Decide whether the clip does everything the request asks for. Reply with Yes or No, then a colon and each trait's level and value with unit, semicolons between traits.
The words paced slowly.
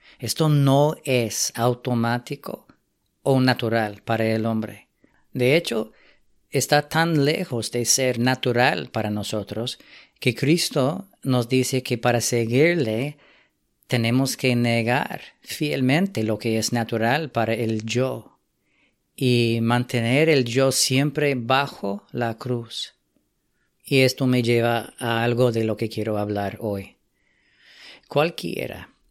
Yes: slow, 120 wpm